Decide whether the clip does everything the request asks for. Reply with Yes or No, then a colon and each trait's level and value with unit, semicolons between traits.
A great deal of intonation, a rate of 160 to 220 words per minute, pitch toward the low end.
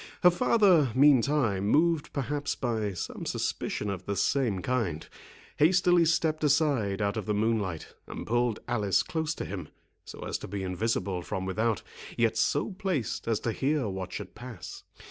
Yes: wide, 6.7 semitones; average, 165 wpm; low, 115 Hz